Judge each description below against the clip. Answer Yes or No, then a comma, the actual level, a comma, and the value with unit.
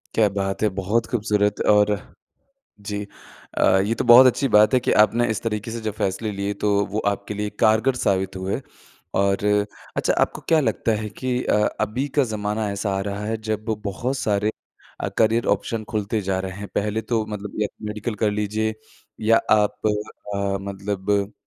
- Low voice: Yes, low, 105 Hz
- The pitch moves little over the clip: Yes, narrow, 1.8 semitones